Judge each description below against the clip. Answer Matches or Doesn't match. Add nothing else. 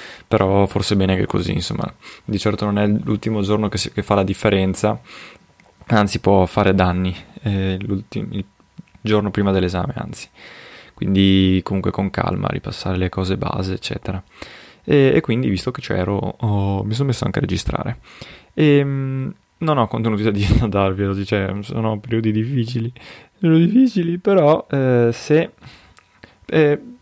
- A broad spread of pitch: Doesn't match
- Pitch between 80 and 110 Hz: Matches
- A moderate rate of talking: Matches